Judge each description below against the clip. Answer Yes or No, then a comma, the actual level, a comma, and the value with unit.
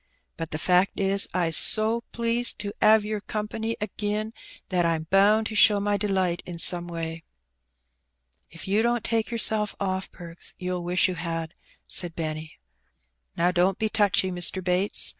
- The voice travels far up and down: No, average, 3.5 semitones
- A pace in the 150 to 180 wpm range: Yes, average, 160 wpm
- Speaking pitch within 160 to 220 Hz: Yes, high, 190 Hz